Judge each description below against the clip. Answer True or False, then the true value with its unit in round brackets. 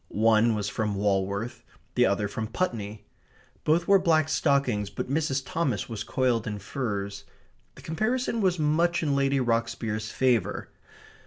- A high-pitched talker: False (120 Hz)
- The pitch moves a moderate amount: False (6.6 semitones)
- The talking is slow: False (145 wpm)